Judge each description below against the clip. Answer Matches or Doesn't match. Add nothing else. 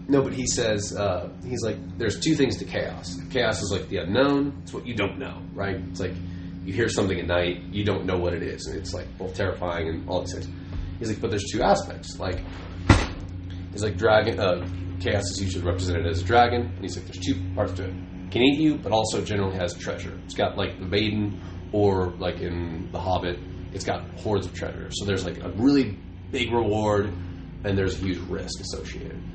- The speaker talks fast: Matches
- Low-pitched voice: Matches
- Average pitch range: Doesn't match